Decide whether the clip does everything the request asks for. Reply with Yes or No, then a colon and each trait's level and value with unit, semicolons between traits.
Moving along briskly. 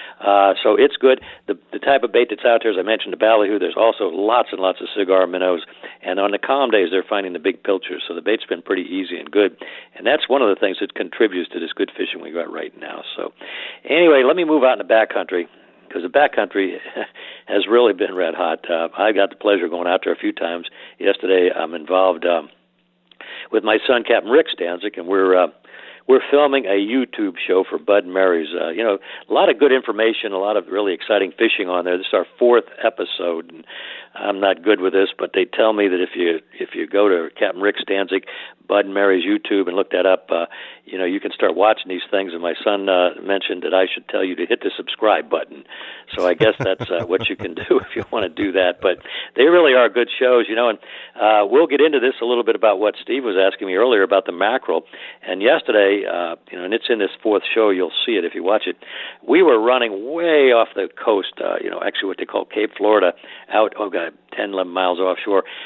Yes: fast, 245 wpm